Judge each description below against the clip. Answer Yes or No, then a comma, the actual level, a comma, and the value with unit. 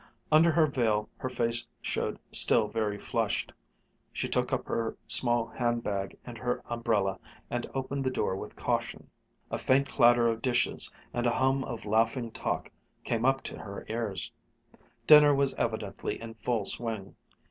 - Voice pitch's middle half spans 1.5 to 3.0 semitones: Yes, average, 2.7 semitones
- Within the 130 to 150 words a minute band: No, average, 160 wpm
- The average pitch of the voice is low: Yes, low, 120 Hz